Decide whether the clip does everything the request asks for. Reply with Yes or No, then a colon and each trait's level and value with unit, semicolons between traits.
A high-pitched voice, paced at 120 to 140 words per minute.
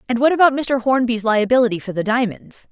No: high, 240 Hz; average, 200 wpm